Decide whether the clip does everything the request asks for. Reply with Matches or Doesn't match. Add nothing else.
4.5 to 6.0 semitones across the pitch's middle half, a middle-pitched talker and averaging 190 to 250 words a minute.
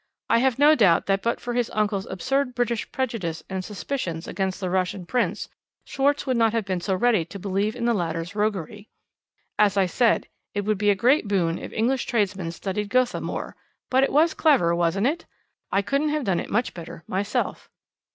Doesn't match